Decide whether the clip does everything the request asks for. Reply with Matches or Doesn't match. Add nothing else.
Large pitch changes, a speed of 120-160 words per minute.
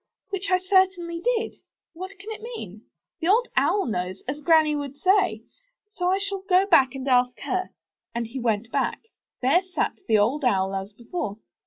Doesn't match